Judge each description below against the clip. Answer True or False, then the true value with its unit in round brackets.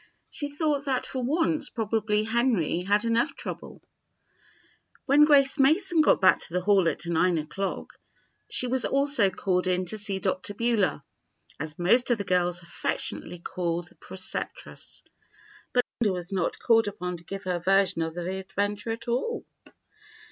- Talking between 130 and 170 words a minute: True (160 wpm)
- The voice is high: True (205 Hz)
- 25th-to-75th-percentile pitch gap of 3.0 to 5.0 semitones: False (5.5 semitones)